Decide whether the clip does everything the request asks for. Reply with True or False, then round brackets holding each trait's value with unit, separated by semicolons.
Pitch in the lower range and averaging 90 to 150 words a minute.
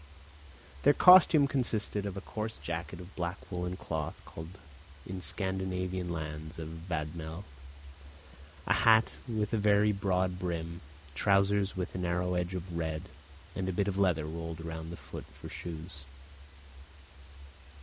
True (90 Hz; 140 wpm)